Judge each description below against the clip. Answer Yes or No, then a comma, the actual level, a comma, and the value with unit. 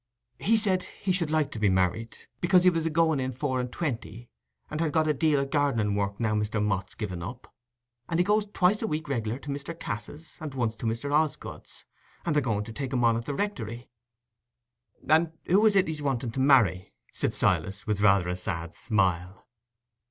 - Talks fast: Yes, fast, 210 wpm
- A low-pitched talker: Yes, low, 130 Hz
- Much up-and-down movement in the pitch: Yes, wide, 6.8 semitones